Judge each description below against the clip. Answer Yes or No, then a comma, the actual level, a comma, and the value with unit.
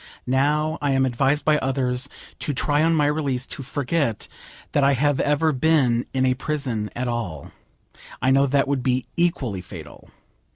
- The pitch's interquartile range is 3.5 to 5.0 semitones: No, average, 2.8 semitones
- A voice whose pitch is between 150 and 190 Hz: No, low, 135 Hz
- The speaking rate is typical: Yes, average, 170 wpm